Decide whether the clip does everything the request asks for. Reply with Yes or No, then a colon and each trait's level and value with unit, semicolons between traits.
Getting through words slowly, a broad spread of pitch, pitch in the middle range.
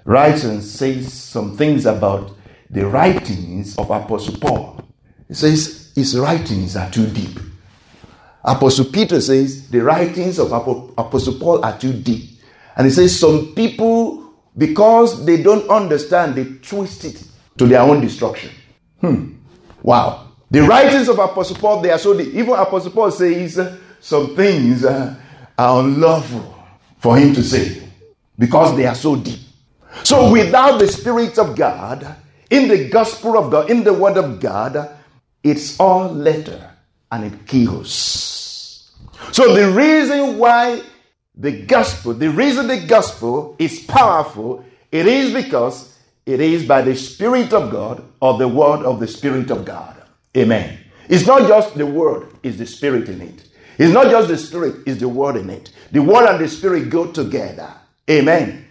No: average, 155 wpm; wide, 7.9 semitones; medium, 145 Hz